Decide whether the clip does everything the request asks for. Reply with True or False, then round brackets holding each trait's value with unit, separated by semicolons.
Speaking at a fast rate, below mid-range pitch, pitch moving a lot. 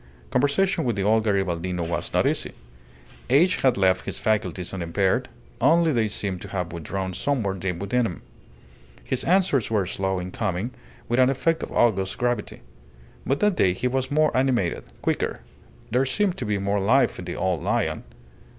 False (175 wpm; 105 Hz; 5.8 semitones)